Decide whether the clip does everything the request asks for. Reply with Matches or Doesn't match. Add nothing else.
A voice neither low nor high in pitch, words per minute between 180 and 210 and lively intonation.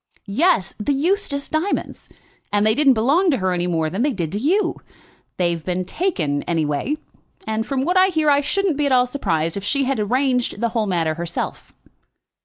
Doesn't match